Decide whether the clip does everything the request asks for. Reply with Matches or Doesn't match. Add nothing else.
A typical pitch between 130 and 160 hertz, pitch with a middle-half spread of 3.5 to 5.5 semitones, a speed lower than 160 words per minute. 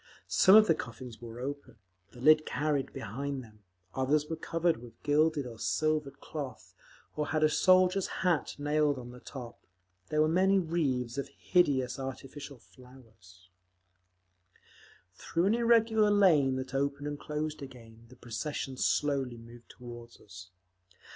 Matches